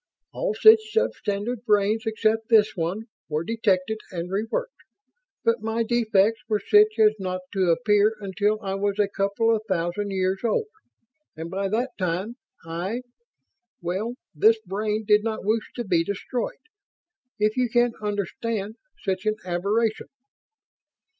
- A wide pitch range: No, average, 2.7 semitones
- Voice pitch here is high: Yes, high, 210 Hz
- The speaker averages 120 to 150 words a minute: Yes, average, 145 wpm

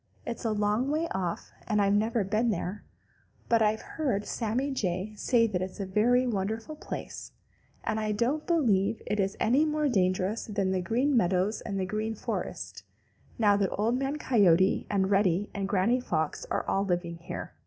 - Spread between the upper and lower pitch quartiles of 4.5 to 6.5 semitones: No, average, 3.7 semitones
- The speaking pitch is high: Yes, high, 210 Hz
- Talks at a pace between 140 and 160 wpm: No, average, 180 wpm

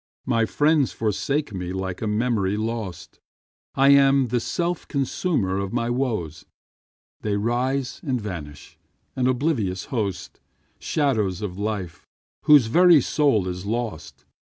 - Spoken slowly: Yes, slow, 130 wpm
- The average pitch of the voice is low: Yes, low, 115 Hz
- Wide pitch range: Yes, wide, 5.9 semitones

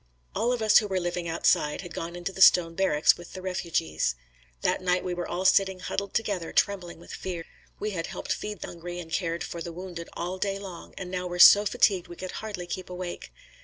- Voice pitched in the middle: Yes, medium, 180 Hz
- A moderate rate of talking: No, fast, 225 wpm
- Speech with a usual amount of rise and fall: No, narrow, 2.0 semitones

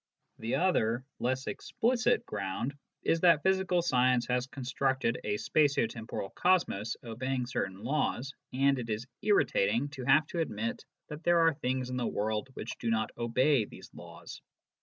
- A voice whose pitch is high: No, low, 130 Hz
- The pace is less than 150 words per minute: No, average, 160 wpm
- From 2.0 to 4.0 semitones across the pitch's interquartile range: No, average, 4.8 semitones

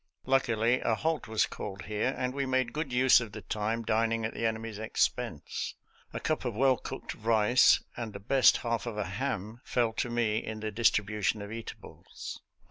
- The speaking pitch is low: Yes, low, 115 Hz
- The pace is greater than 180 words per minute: Yes, average, 190 wpm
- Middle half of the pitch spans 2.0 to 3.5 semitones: Yes, narrow, 2.5 semitones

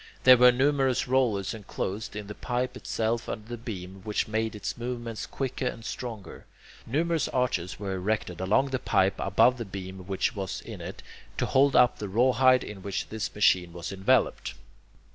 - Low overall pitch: Yes, low, 110 Hz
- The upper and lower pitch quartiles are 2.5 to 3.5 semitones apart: No, average, 4.4 semitones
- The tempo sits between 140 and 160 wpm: No, average, 175 wpm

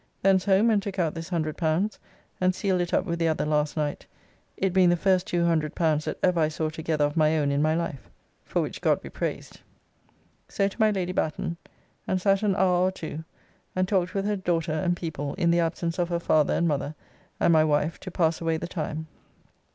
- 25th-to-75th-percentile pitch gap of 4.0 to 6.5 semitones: No, average, 2.9 semitones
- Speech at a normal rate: No, fast, 215 wpm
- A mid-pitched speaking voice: Yes, medium, 170 Hz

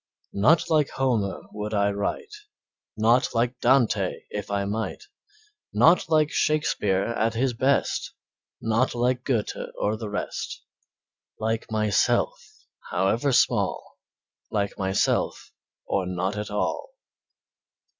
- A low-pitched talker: Yes, low, 110 Hz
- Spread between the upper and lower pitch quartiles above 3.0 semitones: Yes, average, 4.4 semitones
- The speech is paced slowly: Yes, slow, 115 wpm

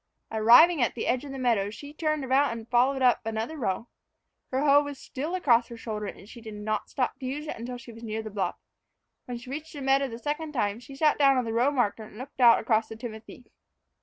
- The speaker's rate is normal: No, fast, 245 wpm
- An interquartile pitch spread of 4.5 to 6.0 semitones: No, average, 3.8 semitones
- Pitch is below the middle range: No, high, 245 Hz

